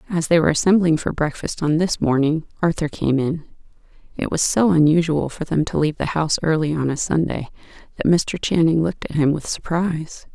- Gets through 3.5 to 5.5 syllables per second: No, 5.8 syllables/s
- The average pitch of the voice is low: No, medium, 160 Hz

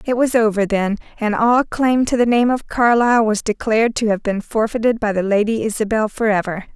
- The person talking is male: No, female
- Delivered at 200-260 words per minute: Yes, fast, 205 wpm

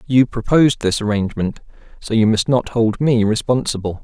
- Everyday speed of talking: Yes, average, 165 wpm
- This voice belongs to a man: Yes, male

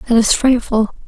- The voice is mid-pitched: No, high, 235 Hz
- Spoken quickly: No, average, 170 wpm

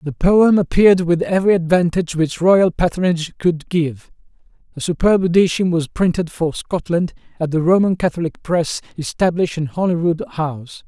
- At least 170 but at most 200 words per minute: No, average, 150 wpm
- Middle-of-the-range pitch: Yes, medium, 170 Hz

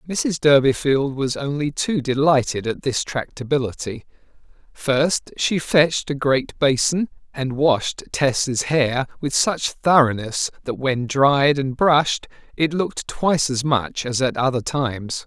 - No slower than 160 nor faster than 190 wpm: No, average, 140 wpm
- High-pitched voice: No, medium, 140 Hz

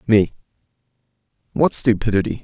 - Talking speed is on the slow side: Yes, slow, 75 wpm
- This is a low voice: Yes, low, 110 Hz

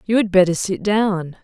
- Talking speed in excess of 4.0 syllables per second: Yes, 4.7 syllables/s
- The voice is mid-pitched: No, high, 195 Hz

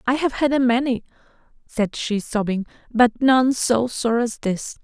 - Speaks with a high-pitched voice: Yes, high, 240 Hz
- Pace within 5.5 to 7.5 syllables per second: No, 4.4 syllables/s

